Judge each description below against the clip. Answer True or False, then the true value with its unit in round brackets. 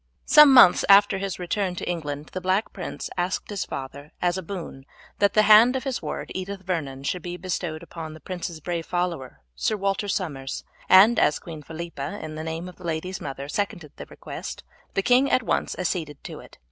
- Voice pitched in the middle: True (180 Hz)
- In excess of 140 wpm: True (200 wpm)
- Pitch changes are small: False (3.9 semitones)